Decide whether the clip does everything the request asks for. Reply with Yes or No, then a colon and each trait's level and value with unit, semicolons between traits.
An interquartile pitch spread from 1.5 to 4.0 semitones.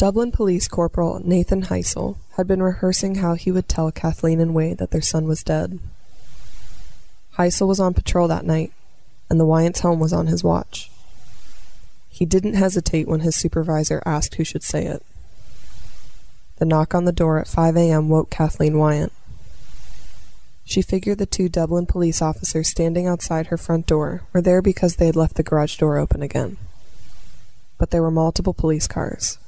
Yes: narrow, 2.4 semitones